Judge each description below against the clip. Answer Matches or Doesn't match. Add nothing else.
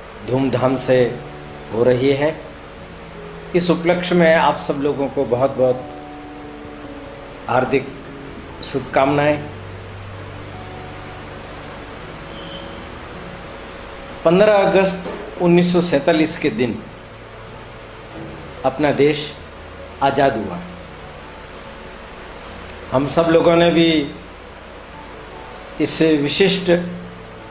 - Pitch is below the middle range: Matches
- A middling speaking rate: Doesn't match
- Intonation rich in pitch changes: Matches